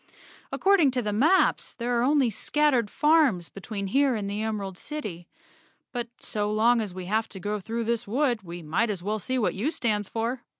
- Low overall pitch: No, high, 225 Hz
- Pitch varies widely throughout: No, average, 4.1 semitones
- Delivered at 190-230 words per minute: Yes, average, 200 wpm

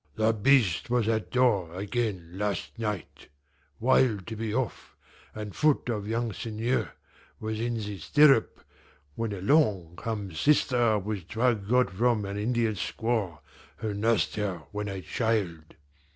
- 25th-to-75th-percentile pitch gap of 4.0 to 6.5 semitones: No, average, 3.0 semitones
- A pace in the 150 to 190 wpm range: No, average, 140 wpm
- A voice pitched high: No, low, 110 Hz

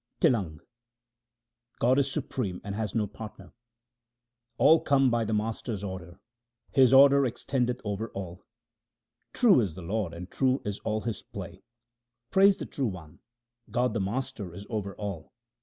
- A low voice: Yes, low, 110 Hz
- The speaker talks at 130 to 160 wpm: Yes, average, 155 wpm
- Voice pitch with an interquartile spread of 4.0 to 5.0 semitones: Yes, average, 4.5 semitones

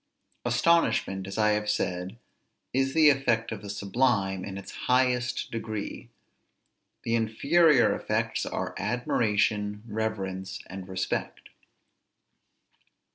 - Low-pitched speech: Yes, low, 110 Hz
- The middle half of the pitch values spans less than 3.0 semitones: No, average, 4.0 semitones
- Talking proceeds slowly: Yes, slow, 105 wpm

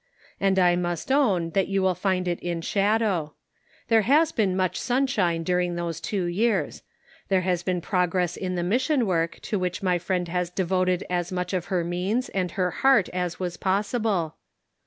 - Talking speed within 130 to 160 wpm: No, average, 185 wpm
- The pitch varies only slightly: Yes, narrow, 2.3 semitones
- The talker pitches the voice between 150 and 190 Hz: Yes, medium, 185 Hz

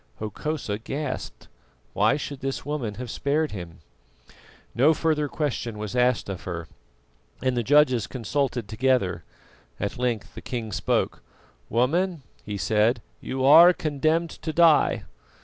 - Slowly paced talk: Yes, slow, 130 wpm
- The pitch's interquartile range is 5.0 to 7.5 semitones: Yes, wide, 5.6 semitones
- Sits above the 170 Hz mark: No, low, 130 Hz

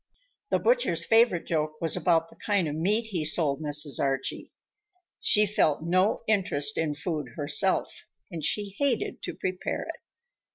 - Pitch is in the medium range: Yes, medium, 165 Hz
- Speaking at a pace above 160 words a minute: No, average, 155 wpm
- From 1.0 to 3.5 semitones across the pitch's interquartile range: No, average, 5.2 semitones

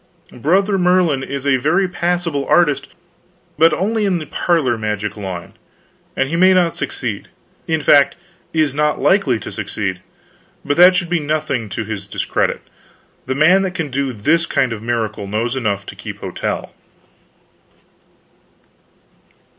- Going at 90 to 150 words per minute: Yes, average, 145 wpm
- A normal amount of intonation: No, wide, 7.1 semitones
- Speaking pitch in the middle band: Yes, medium, 145 Hz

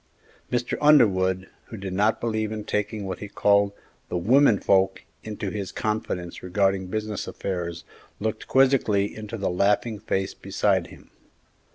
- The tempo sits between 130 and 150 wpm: Yes, average, 145 wpm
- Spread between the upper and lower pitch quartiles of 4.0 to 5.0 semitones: No, narrow, 2.4 semitones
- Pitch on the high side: No, low, 105 Hz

